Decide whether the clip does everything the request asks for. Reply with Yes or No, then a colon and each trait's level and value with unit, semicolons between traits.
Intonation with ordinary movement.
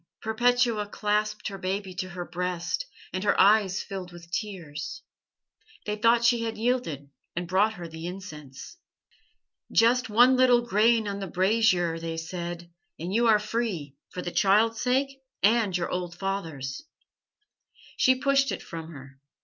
Yes: average, 4.8 semitones